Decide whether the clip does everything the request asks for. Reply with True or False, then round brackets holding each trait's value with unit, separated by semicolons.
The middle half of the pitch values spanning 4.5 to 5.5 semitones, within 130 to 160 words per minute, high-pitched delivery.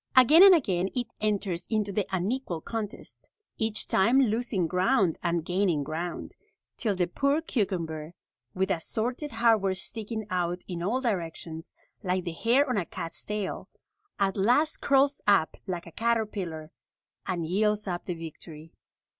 True (4.9 semitones; 145 wpm; 195 Hz)